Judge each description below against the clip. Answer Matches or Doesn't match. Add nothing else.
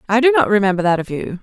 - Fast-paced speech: Matches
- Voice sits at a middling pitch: Doesn't match